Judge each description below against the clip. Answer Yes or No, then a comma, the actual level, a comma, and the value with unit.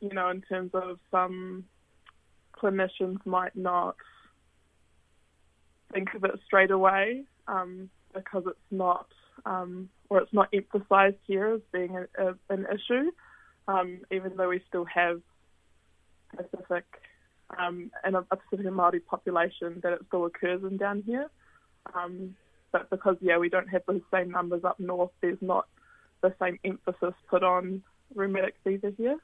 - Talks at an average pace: Yes, average, 150 wpm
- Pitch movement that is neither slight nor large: No, narrow, 1.5 semitones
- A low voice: No, medium, 185 Hz